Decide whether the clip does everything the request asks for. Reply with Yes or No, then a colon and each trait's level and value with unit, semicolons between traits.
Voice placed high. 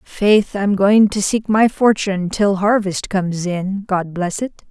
Yes: high, 200 Hz